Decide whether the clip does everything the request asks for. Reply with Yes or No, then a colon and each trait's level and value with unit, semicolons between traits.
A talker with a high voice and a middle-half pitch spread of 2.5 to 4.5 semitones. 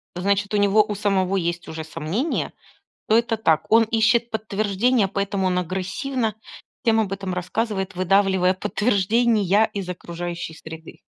Yes: high, 200 Hz; average, 3.2 semitones